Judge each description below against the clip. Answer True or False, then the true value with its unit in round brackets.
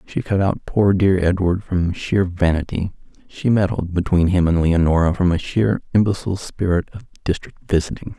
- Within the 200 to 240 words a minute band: False (170 wpm)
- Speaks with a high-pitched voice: False (90 Hz)